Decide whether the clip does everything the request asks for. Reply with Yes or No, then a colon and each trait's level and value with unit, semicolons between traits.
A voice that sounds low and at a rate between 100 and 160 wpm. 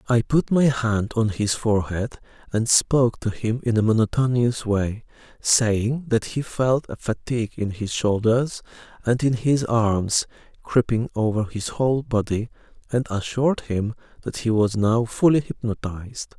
Yes: low, 115 Hz; average, 155 wpm